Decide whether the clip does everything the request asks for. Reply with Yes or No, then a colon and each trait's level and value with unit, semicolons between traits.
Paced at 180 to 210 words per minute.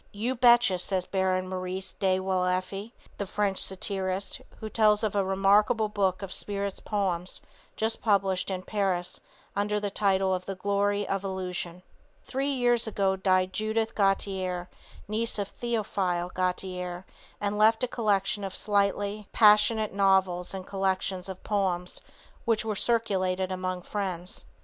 No: average, 145 wpm